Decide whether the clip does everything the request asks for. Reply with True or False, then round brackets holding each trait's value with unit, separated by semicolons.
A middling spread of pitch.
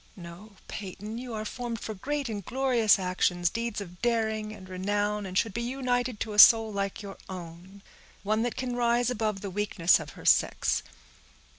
True (3.6 semitones)